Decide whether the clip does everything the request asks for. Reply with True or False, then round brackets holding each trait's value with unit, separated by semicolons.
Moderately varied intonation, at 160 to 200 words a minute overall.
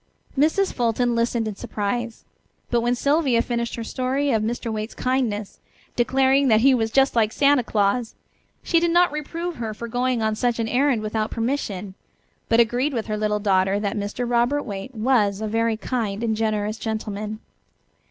True (3.1 semitones; 175 wpm)